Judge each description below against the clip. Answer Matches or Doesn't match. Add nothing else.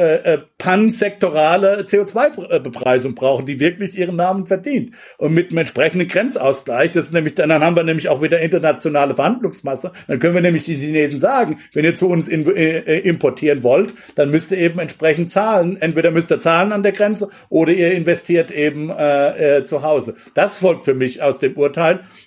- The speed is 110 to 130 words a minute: Doesn't match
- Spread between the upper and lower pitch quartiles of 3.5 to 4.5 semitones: Matches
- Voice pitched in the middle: Matches